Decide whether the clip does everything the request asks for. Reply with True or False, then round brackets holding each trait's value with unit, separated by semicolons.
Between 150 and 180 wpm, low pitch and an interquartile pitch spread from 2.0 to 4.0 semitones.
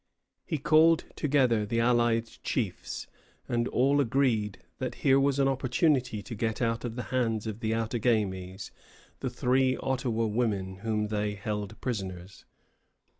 False (140 wpm; 115 Hz; 3.5 semitones)